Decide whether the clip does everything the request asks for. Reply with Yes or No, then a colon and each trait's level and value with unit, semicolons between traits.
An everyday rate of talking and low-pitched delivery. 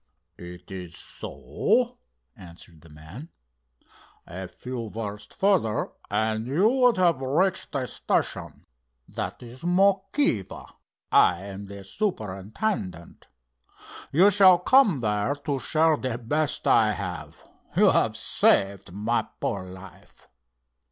No: slow, 115 wpm; low, 115 Hz